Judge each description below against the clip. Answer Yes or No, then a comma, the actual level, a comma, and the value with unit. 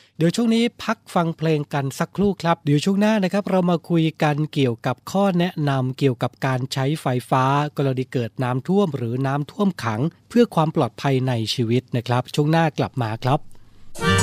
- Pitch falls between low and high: Yes, medium, 145 Hz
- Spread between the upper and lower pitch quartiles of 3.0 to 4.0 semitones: No, average, 5.0 semitones